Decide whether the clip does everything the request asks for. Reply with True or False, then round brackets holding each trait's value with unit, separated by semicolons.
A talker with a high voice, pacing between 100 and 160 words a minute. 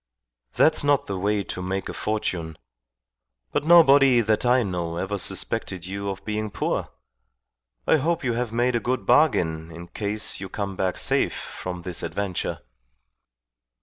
False (100 Hz; 155 wpm)